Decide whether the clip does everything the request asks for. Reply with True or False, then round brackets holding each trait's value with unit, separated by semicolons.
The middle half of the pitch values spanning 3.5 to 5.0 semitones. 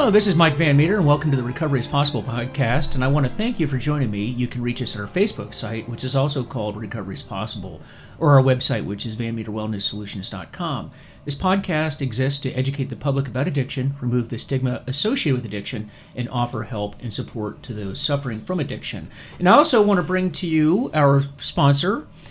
True (4.2 semitones)